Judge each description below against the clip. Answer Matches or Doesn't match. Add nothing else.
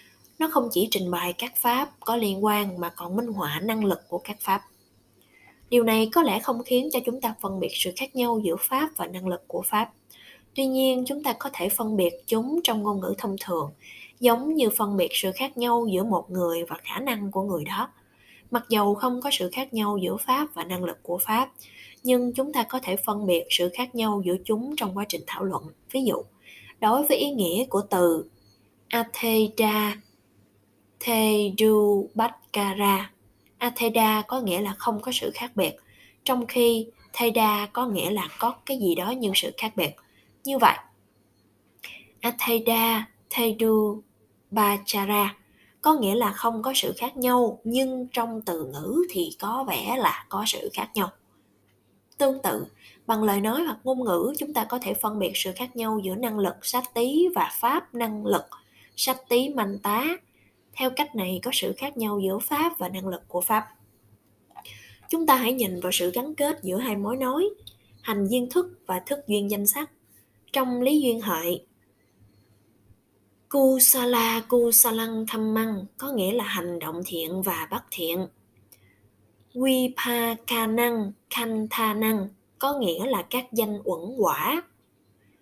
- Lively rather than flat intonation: Doesn't match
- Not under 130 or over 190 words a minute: Matches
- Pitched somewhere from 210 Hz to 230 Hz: Matches